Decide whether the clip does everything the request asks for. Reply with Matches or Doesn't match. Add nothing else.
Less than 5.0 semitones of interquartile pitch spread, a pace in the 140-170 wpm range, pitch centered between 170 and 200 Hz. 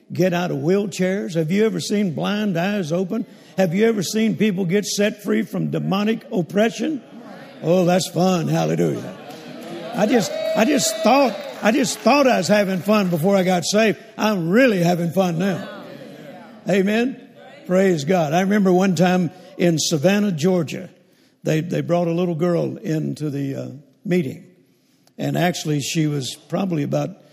Matches